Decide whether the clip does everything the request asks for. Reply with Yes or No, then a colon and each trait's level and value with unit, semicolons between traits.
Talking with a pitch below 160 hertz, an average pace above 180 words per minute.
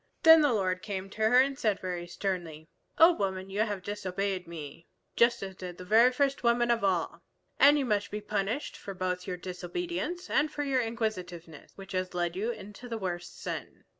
No: high, 200 Hz; average, 195 wpm